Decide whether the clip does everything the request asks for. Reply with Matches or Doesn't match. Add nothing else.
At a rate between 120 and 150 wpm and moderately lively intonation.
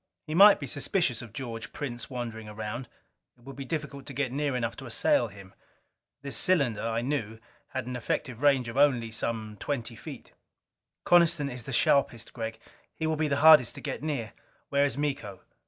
Doesn't match